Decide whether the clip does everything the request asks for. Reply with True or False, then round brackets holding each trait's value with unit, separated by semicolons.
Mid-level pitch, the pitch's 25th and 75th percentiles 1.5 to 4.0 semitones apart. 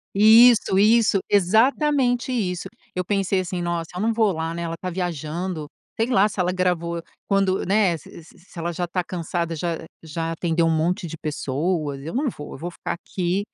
True (180 Hz; 3.4 semitones)